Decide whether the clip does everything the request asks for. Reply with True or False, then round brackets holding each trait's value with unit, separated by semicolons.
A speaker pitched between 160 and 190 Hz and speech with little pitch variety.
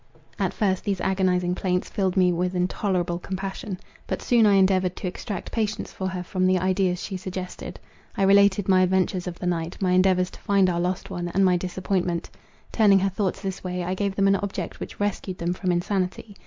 True (185 Hz; 1.4 semitones)